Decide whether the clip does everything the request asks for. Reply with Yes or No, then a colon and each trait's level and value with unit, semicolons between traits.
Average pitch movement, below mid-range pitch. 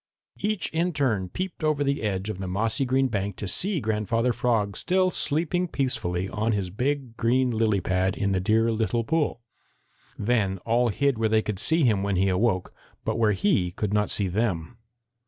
Yes: average, 5.0 semitones; low, 110 Hz